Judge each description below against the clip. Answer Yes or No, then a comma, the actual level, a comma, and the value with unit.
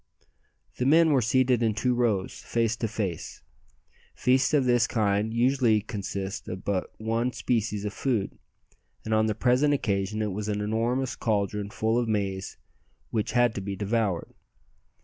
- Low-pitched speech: Yes, low, 110 Hz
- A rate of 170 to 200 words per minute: No, average, 160 wpm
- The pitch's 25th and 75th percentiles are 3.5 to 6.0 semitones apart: No, average, 3.1 semitones